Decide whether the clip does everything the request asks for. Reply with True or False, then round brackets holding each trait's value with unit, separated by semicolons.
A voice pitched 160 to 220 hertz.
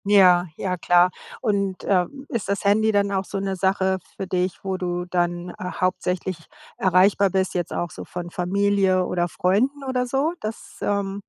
True (190 Hz)